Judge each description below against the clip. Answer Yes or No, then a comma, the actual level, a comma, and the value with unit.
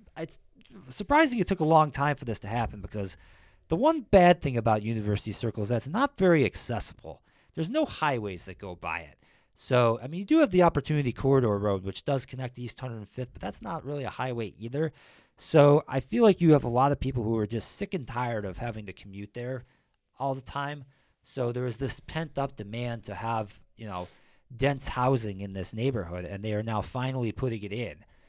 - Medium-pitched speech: No, low, 120 Hz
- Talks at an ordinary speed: No, fast, 215 wpm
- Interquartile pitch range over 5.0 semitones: Yes, wide, 5.4 semitones